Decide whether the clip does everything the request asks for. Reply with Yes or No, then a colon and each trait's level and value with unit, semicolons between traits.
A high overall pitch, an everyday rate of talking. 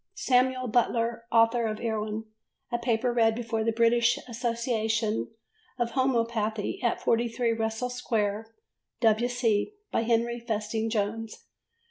No: high, 230 Hz; slow, 115 wpm